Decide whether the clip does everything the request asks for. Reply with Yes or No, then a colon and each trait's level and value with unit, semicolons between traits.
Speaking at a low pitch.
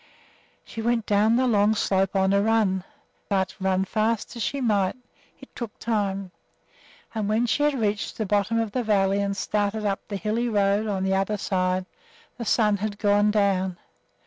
No: high, 205 Hz